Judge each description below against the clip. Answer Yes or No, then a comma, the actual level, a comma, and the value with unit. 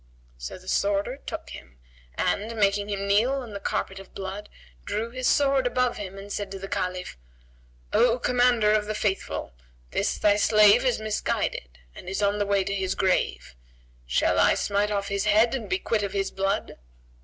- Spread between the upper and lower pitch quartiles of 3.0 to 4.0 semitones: No, narrow, 2.6 semitones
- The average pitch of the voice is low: No, high, 205 Hz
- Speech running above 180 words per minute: Yes, average, 190 wpm